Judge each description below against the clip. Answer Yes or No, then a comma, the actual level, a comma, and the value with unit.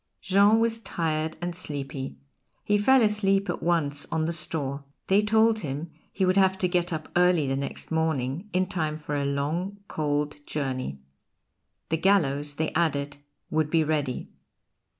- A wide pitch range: No, average, 4.5 semitones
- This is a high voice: No, medium, 160 Hz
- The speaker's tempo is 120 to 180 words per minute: Yes, average, 160 wpm